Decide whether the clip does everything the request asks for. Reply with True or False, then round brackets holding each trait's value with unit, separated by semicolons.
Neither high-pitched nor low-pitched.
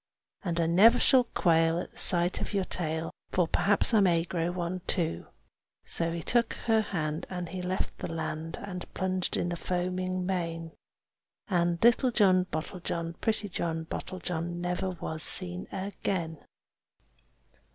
True (175 Hz)